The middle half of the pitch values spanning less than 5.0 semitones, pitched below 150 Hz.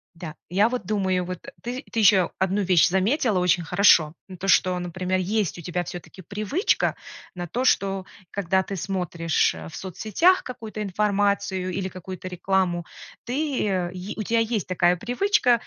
No: average, 3.1 semitones; high, 190 Hz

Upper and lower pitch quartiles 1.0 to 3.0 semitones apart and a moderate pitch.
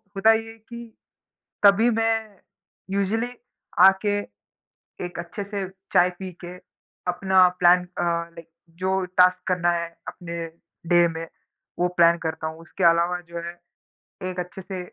Yes: average, 2.7 semitones; medium, 180 Hz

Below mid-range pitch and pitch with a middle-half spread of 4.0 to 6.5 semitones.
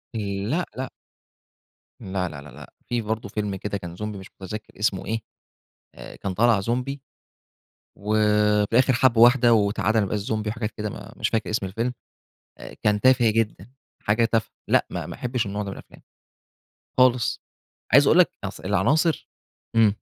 No: low, 110 Hz; average, 2.7 semitones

